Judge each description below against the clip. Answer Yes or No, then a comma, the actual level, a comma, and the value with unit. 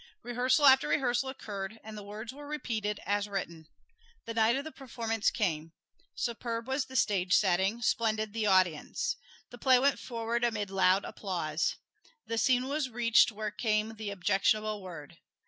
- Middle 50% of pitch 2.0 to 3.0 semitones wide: No, average, 3.5 semitones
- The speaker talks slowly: No, average, 160 wpm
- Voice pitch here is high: Yes, high, 220 Hz